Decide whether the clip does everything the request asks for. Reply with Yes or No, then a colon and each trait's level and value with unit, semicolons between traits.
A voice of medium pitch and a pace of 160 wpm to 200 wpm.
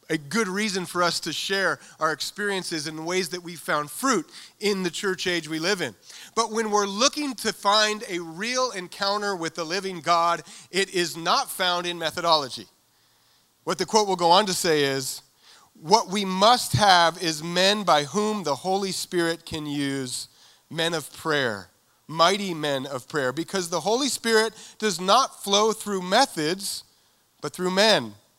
Yes: medium, 180 Hz; average, 175 wpm